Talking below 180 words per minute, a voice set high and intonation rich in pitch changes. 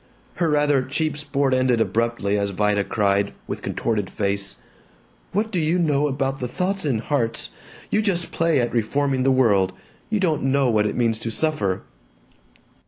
No: average, 170 wpm; low, 130 Hz; wide, 5.8 semitones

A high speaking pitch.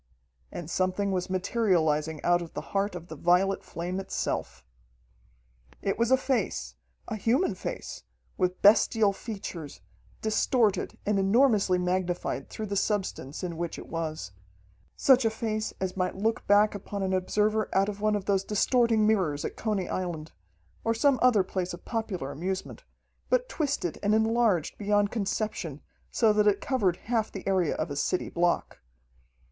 Yes: high, 195 Hz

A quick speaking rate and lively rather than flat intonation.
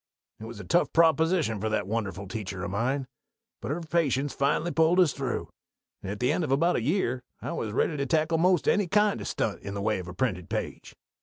Yes: fast, 235 wpm; wide, 7.5 semitones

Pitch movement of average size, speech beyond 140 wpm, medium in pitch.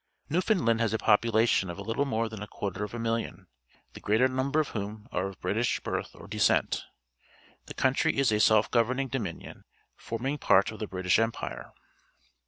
No: average, 3.7 semitones; average, 180 wpm; low, 115 Hz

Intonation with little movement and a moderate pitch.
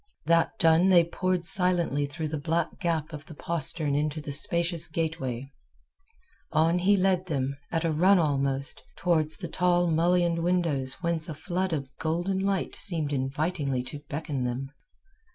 No: average, 3.3 semitones; medium, 165 Hz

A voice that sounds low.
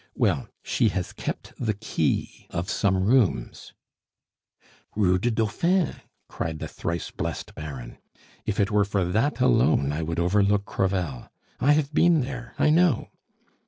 Yes: low, 105 Hz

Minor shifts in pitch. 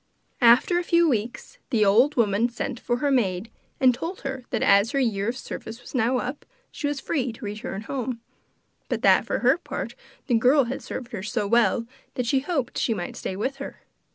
No: average, 3.5 semitones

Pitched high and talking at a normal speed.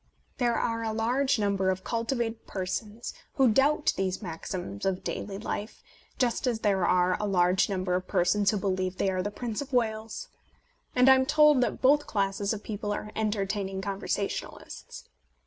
Yes: high, 210 Hz; average, 170 wpm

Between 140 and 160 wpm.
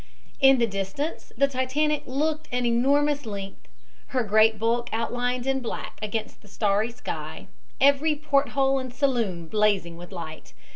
Yes: average, 150 wpm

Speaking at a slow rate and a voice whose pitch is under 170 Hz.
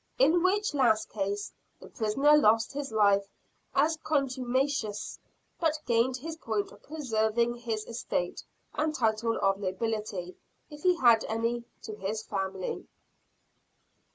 No: slow, 125 wpm; high, 230 Hz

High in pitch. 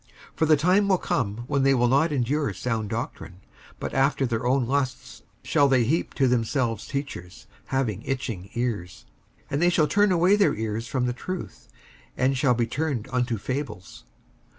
No: low, 130 Hz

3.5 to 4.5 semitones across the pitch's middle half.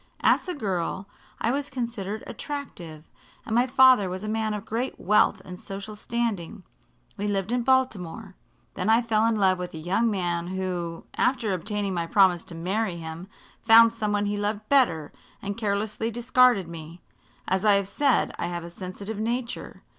Yes: average, 4.1 semitones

